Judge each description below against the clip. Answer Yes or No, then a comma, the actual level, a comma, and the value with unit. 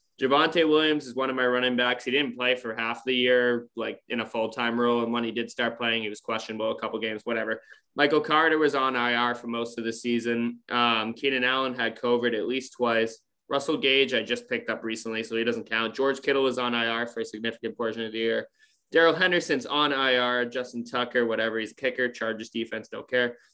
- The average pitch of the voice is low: Yes, low, 120 Hz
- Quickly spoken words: Yes, fast, 225 wpm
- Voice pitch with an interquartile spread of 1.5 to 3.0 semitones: Yes, narrow, 2.4 semitones